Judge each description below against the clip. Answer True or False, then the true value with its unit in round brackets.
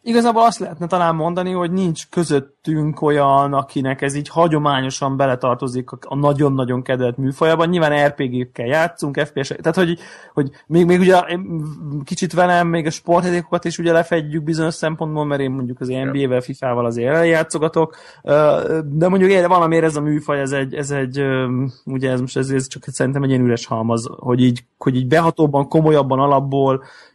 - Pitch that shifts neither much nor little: True (3.6 semitones)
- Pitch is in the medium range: True (145 Hz)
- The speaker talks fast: True (165 wpm)